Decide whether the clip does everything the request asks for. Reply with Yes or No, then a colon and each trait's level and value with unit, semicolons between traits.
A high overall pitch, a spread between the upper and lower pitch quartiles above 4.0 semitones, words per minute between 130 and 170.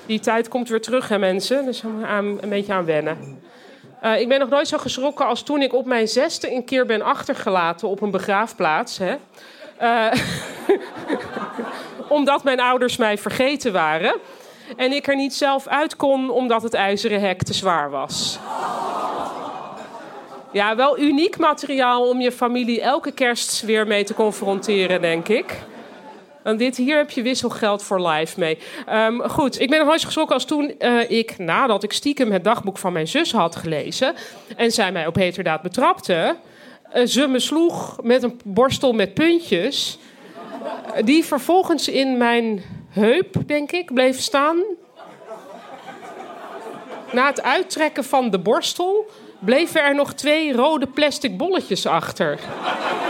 Yes: very high, 250 Hz; average, 5.3 semitones; average, 155 wpm